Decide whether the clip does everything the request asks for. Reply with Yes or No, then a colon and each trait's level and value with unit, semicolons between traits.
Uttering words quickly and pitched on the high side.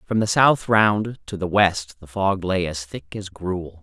No: fast, 220 wpm; very low, 95 Hz